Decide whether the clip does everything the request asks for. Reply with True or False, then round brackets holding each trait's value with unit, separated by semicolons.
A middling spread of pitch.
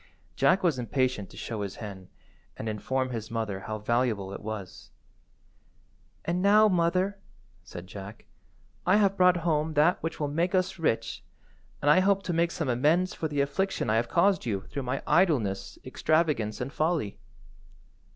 False (8.1 semitones)